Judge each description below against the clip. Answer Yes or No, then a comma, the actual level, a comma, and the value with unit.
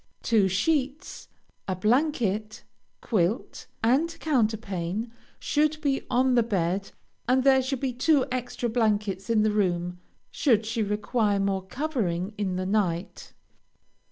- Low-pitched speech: No, high, 220 Hz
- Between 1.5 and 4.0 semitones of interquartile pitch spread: No, average, 4.8 semitones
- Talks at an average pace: No, slow, 130 wpm